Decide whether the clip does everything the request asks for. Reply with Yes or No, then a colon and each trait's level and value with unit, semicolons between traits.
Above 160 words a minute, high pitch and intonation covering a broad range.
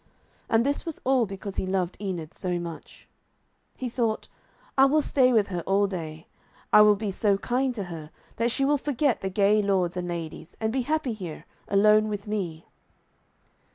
No: average, 185 wpm; high, 205 Hz; average, 4.7 semitones